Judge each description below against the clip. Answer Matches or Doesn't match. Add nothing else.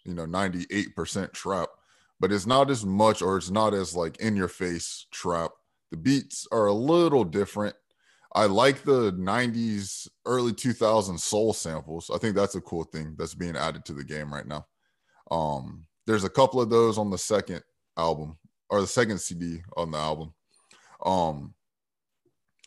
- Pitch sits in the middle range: Doesn't match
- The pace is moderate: Matches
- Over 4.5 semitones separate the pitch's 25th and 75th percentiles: Matches